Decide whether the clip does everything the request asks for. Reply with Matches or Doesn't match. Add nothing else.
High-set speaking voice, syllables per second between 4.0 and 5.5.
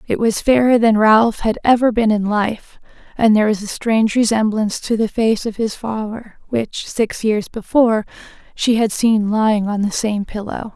Matches